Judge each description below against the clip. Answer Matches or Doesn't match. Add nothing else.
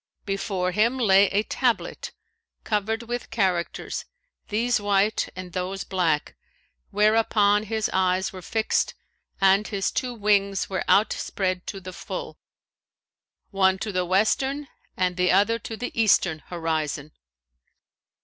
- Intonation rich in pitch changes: Doesn't match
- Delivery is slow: Matches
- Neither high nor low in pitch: Doesn't match